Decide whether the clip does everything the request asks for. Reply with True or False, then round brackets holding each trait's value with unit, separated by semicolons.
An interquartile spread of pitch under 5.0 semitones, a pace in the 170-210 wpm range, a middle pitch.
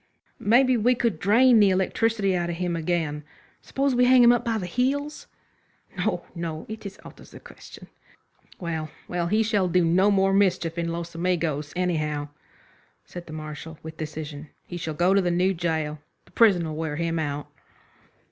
True (4.4 semitones; 180 wpm; 175 Hz)